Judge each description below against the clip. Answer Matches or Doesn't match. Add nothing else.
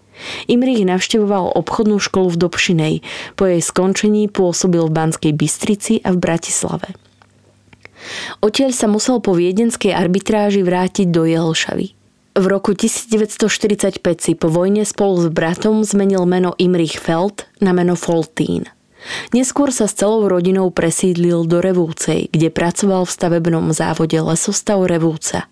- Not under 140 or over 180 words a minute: Doesn't match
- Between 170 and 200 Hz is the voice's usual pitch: Matches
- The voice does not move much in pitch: Doesn't match